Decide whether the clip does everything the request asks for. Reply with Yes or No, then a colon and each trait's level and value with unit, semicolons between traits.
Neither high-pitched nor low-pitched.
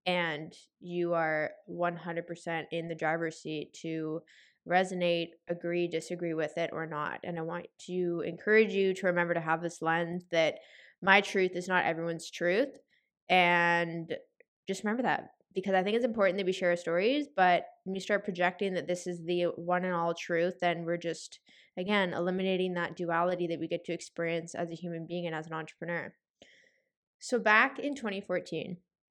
Yes: medium, 175 Hz